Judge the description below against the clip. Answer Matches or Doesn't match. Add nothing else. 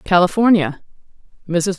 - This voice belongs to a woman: Matches